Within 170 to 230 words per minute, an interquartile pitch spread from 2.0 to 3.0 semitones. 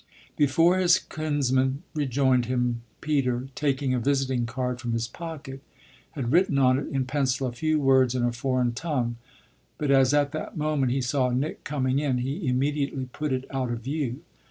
Yes: average, 180 wpm; narrow, 2.6 semitones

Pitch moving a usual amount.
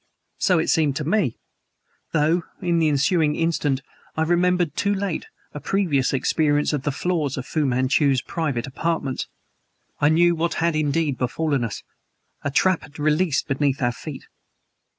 Yes: average, 3.4 semitones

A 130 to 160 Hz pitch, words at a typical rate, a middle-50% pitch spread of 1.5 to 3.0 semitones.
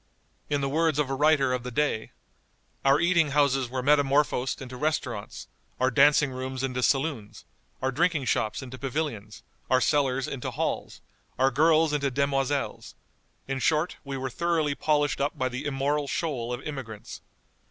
Yes: low, 135 Hz; average, 160 wpm; narrow, 2.5 semitones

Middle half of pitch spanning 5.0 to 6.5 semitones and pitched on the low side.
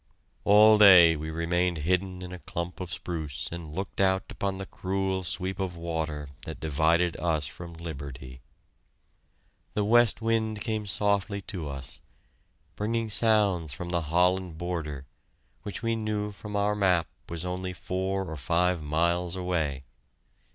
No: average, 3.3 semitones; very low, 90 Hz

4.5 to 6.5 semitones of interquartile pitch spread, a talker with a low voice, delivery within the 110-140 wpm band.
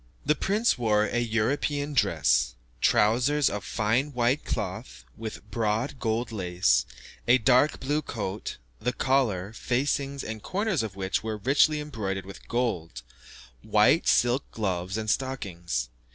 Yes: wide, 5.5 semitones; low, 115 Hz; slow, 135 wpm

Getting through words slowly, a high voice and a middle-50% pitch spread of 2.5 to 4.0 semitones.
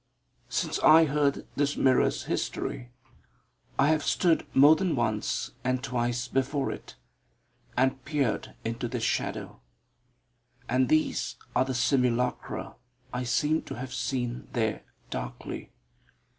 No: slow, 120 wpm; low, 130 Hz; average, 2.8 semitones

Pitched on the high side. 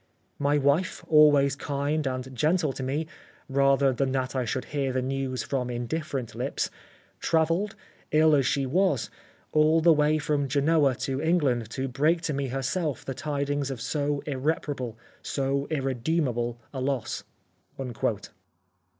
No: medium, 140 Hz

